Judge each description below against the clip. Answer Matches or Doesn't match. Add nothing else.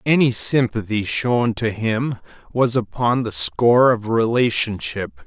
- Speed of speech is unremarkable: Doesn't match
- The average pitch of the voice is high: Doesn't match